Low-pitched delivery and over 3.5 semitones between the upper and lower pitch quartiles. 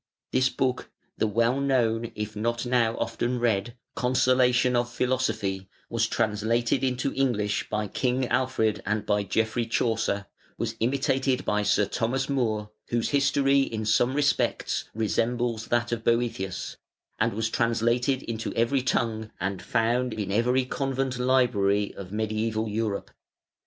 No: low, 115 Hz; average, 2.7 semitones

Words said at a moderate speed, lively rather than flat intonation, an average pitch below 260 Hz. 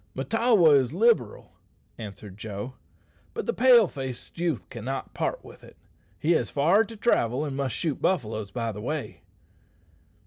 Yes: average, 150 wpm; wide, 8.5 semitones; medium, 140 Hz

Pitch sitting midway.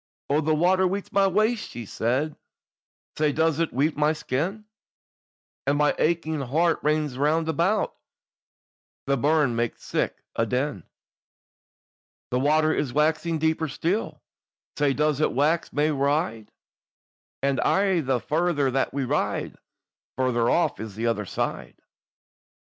Yes: medium, 150 Hz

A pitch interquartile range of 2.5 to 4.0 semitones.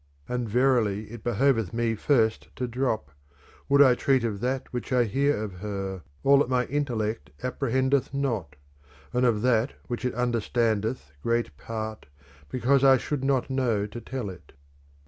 Yes: average, 3.3 semitones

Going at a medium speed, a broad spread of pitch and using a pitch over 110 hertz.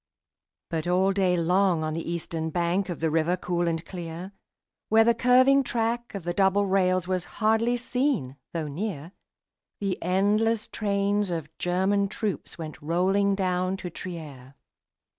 No: average, 150 wpm; average, 3.2 semitones; medium, 185 Hz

